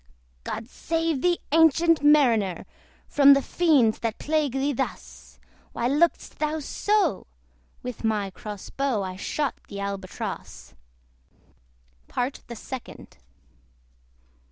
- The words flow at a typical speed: No, slow, 110 wpm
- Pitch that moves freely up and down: Yes, wide, 5.9 semitones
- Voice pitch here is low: No, very high, 270 Hz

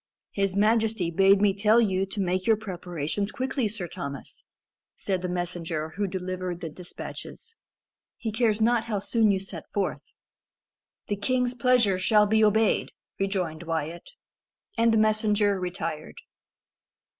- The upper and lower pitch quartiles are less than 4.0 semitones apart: Yes, average, 3.3 semitones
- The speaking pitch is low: No, high, 200 Hz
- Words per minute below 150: Yes, average, 140 wpm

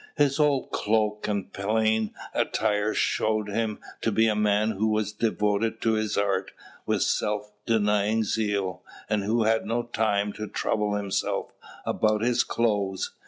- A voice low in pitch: Yes, low, 105 Hz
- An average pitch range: No, narrow, 1.3 semitones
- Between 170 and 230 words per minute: No, average, 150 wpm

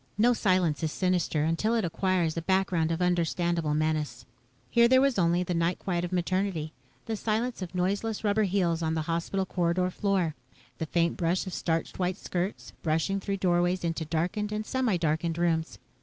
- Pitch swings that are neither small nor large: Yes, average, 3.0 semitones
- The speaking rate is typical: Yes, average, 180 wpm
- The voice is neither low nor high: Yes, medium, 175 Hz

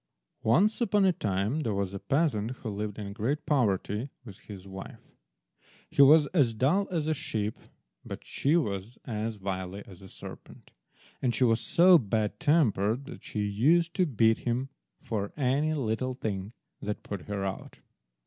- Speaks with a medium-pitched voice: No, low, 115 Hz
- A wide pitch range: Yes, wide, 6.4 semitones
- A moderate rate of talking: Yes, average, 170 wpm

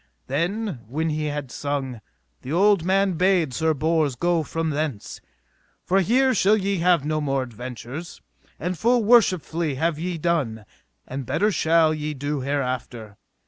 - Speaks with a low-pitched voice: No, medium, 160 Hz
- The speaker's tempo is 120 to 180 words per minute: Yes, average, 150 wpm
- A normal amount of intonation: Yes, average, 4.6 semitones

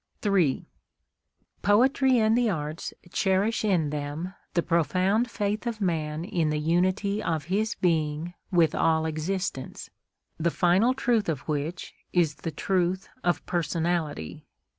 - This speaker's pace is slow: Yes, slow, 130 wpm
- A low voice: No, medium, 175 Hz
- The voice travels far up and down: No, average, 4.3 semitones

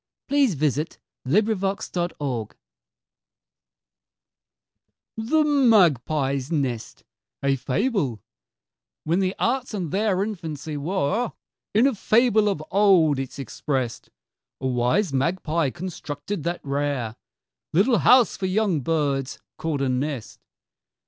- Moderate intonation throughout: No, wide, 7.0 semitones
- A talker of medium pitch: Yes, medium, 165 Hz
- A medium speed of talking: No, slow, 100 wpm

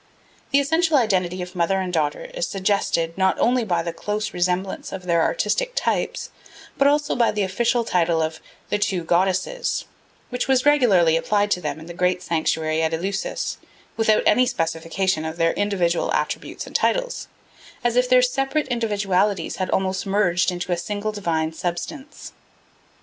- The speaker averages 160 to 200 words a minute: Yes, average, 165 wpm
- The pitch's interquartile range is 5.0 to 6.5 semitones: Yes, wide, 5.6 semitones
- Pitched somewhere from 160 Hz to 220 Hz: Yes, high, 190 Hz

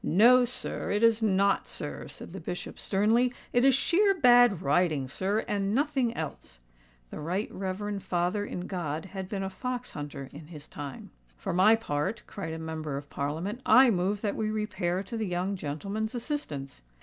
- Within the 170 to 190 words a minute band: Yes, average, 175 wpm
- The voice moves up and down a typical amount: No, wide, 5.7 semitones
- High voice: Yes, high, 195 Hz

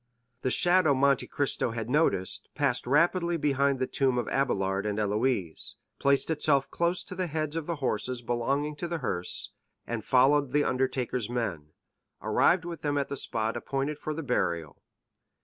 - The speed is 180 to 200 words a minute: No, average, 165 wpm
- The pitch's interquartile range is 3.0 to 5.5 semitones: Yes, average, 4.2 semitones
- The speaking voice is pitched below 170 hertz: Yes, low, 135 Hz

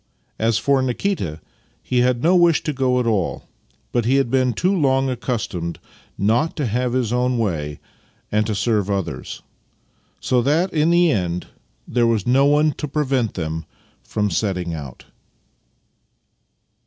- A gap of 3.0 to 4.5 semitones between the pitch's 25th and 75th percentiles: No, average, 5.2 semitones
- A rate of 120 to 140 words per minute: No, average, 155 wpm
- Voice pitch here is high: No, low, 120 Hz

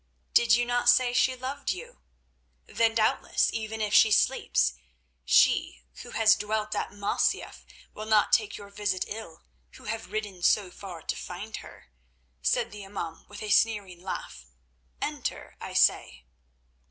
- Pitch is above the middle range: Yes, high, 210 Hz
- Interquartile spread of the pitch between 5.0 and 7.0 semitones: No, average, 2.9 semitones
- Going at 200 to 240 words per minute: No, average, 155 wpm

